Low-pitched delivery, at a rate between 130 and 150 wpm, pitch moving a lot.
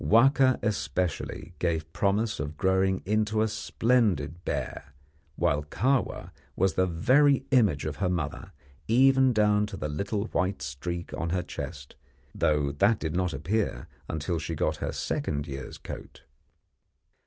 Yes: very low, 95 Hz; average, 140 wpm; wide, 5.8 semitones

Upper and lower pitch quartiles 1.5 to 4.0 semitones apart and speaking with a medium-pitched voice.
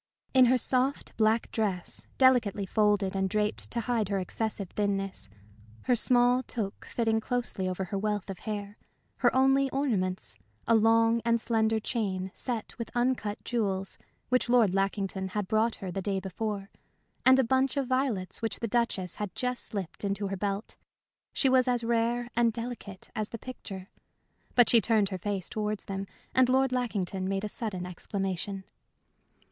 No: average, 3.7 semitones; high, 215 Hz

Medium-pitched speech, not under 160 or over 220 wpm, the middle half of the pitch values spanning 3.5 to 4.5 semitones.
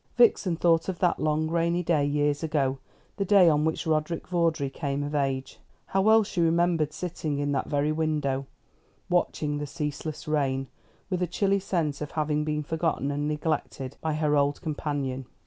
No: medium, 155 Hz; average, 175 wpm; average, 2.7 semitones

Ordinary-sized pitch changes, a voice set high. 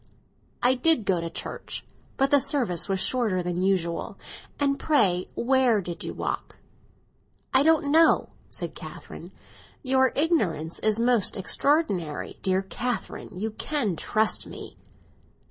No: wide, 6.9 semitones; high, 225 Hz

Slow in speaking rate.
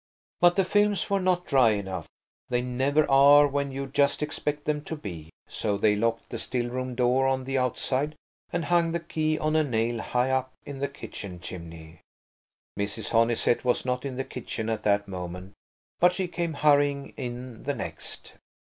No: average, 185 wpm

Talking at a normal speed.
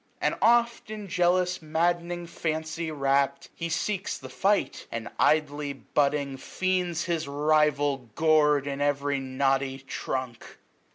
No: slow, 120 wpm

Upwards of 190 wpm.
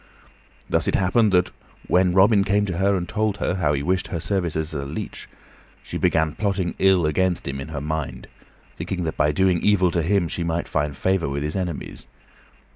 Yes: average, 200 wpm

